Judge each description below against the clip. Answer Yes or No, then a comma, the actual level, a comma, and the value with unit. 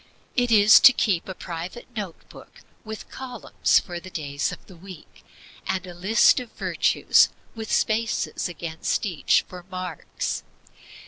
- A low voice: No, medium, 185 Hz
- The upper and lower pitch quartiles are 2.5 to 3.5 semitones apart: No, average, 4.0 semitones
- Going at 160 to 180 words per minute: No, average, 145 wpm